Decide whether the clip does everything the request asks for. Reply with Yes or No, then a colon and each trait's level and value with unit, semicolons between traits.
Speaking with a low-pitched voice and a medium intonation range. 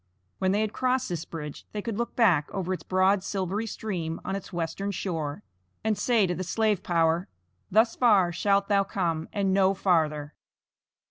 No: high, 190 Hz; average, 3.3 semitones